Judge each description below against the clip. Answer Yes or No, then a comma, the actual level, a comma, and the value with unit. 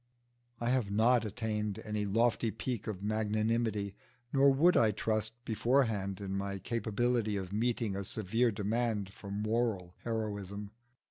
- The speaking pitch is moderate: No, low, 110 Hz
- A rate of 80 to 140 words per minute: Yes, slow, 135 wpm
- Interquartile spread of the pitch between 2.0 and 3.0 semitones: Yes, narrow, 2.5 semitones